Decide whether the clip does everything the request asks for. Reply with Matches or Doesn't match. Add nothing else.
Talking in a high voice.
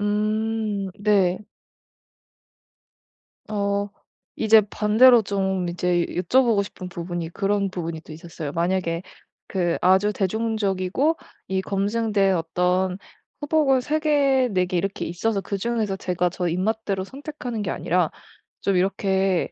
Matches